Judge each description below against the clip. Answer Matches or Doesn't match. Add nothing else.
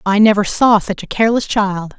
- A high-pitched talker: Matches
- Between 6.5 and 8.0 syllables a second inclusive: Doesn't match